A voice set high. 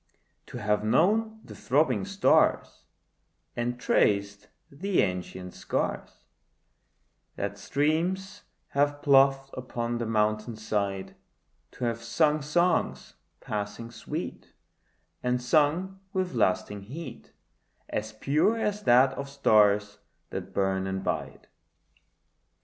No: low, 125 Hz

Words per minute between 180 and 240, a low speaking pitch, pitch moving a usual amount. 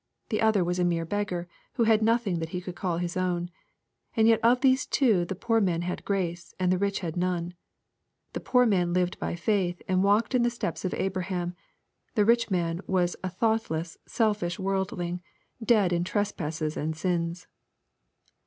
No: average, 190 wpm; medium, 185 Hz; average, 3.5 semitones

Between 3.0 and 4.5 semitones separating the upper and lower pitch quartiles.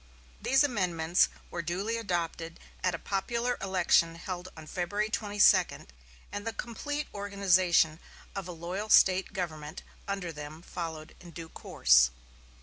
Yes: average, 3.5 semitones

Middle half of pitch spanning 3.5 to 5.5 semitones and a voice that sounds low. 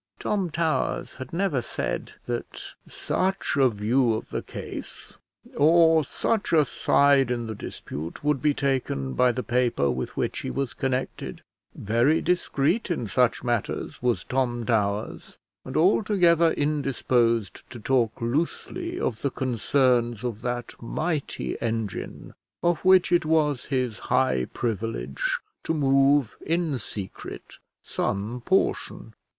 Yes: average, 4.9 semitones; low, 130 Hz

